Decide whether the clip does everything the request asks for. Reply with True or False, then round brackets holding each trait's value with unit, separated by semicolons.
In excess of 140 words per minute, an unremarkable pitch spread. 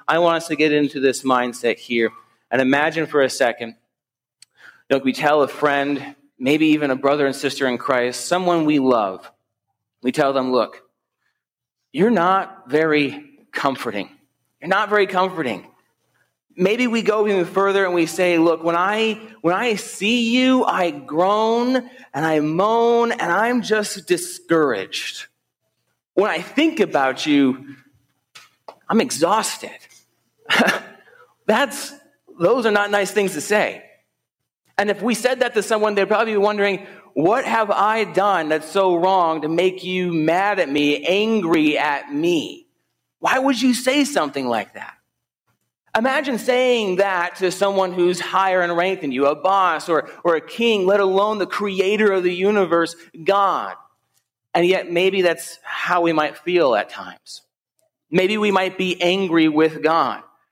False (155 wpm; 5.8 semitones)